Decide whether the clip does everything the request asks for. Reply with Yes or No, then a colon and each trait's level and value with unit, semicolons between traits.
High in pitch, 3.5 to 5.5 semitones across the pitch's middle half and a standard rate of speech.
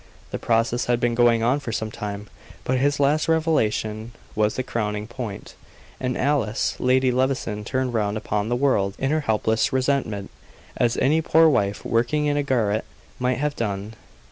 No: low, 120 Hz; average, 3.9 semitones; average, 170 wpm